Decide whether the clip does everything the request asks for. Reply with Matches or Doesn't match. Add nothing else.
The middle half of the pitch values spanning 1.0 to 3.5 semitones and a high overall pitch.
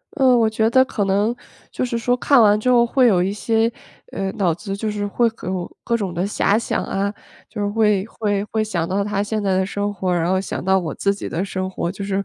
Matches